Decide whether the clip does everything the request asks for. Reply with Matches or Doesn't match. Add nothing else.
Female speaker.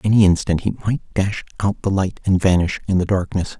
Doesn't match